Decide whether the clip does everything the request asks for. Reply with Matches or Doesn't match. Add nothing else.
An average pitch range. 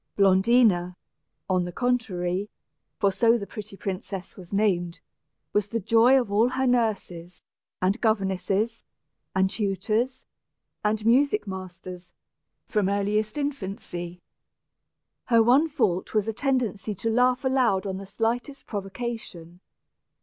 Matches